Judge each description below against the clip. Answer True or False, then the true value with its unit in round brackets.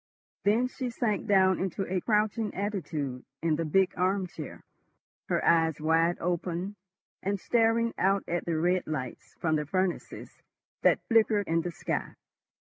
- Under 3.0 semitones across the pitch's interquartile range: False (3.8 semitones)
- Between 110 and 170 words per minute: True (150 wpm)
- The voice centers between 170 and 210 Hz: True (185 Hz)